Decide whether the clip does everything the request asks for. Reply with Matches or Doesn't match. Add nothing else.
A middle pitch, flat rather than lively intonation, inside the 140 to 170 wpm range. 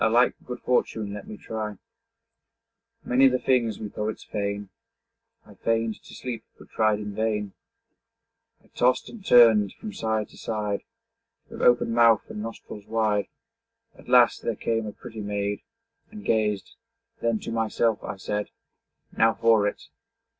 Doesn't match